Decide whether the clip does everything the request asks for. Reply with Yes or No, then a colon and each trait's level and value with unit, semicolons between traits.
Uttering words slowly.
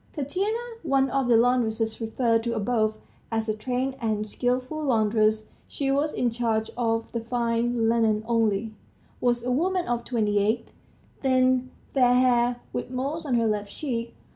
No: average, 160 wpm